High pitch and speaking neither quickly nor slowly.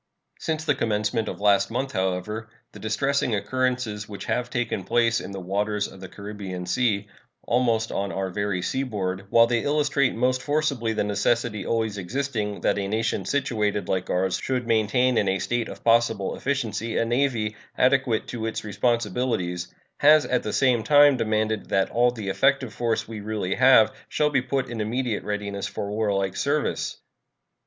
No: low, 110 Hz; average, 170 wpm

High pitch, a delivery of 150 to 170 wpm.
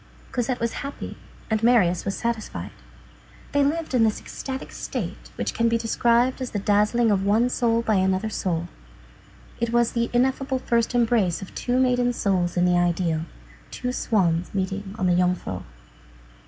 Yes: high, 225 Hz; average, 165 wpm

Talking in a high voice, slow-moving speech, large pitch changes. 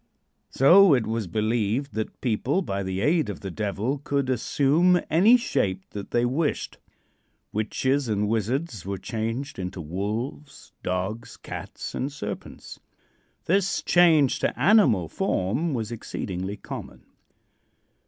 No: low, 115 Hz; slow, 125 wpm; wide, 6.1 semitones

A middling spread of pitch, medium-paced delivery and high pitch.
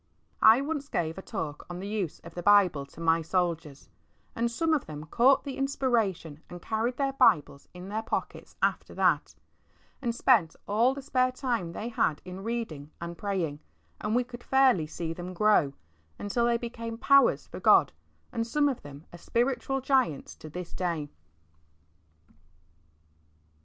No: wide, 6.8 semitones; average, 170 wpm; high, 210 Hz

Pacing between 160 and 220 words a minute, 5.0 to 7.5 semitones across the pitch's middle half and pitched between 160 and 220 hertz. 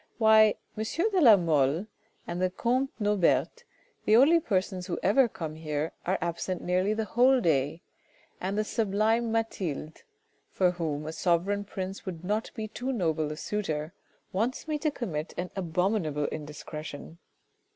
No: average, 150 wpm; average, 5.3 semitones; high, 190 Hz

